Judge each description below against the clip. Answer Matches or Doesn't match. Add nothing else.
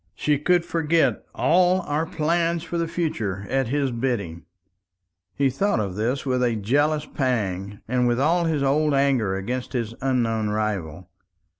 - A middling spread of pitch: Doesn't match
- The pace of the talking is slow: Doesn't match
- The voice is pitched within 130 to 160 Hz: Matches